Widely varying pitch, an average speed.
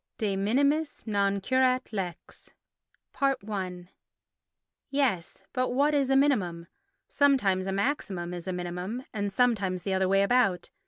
No: wide, 5.7 semitones; slow, 130 wpm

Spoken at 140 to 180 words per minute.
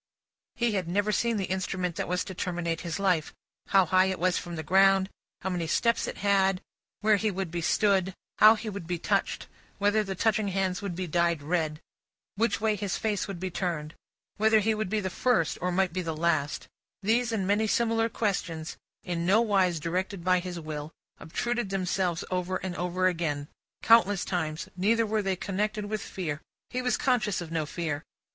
No: average, 195 wpm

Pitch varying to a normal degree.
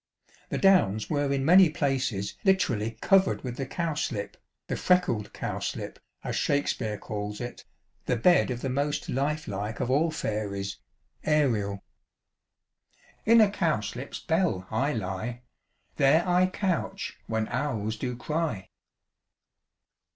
No: wide, 6.9 semitones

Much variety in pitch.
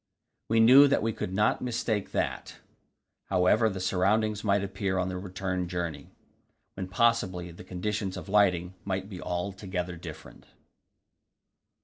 No: average, 2.7 semitones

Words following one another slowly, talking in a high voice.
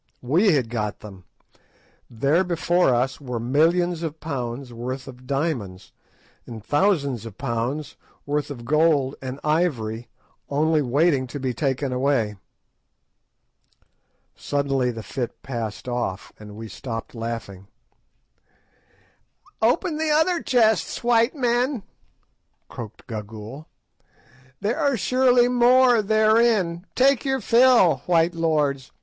No: slow, 115 wpm; medium, 145 Hz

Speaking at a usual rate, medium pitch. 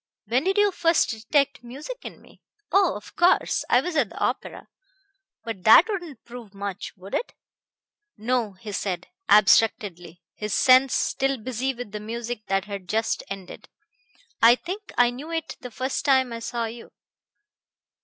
No: average, 165 wpm; high, 240 Hz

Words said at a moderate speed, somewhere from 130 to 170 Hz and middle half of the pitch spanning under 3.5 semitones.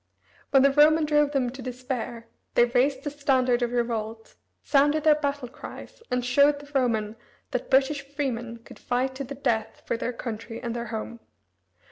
No: average, 175 wpm; very high, 255 Hz; average, 3.1 semitones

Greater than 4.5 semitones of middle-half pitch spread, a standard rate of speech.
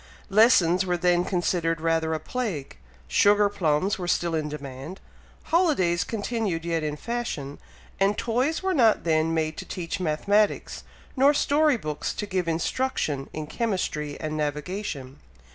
Yes: average, 5.3 semitones; average, 145 wpm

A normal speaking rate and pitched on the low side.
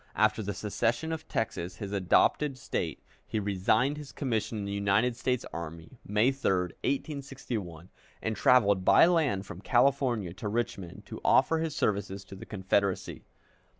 Yes: average, 150 wpm; low, 105 Hz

